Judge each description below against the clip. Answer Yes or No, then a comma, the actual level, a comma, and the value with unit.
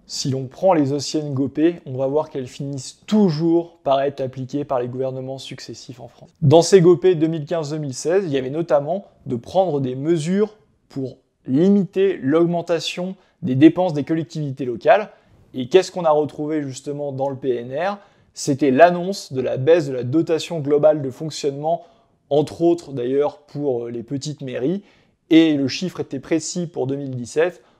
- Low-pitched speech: No, medium, 150 Hz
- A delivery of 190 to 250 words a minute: No, average, 160 wpm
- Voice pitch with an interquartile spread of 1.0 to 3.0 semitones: No, average, 3.9 semitones